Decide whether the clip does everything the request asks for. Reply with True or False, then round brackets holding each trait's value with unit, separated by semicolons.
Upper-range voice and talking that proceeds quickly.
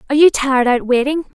True (270 Hz; 215 wpm)